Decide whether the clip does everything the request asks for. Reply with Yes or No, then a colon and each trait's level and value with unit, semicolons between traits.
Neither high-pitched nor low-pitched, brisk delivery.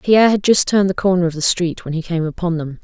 Yes: medium, 175 Hz; fast, 295 wpm